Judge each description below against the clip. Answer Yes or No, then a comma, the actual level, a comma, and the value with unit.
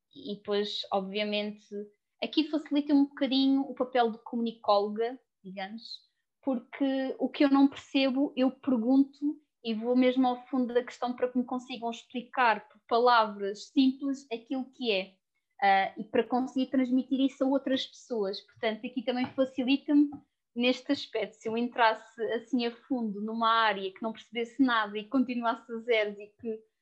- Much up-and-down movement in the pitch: No, average, 3.3 semitones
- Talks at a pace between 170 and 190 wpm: No, average, 160 wpm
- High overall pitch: Yes, high, 245 Hz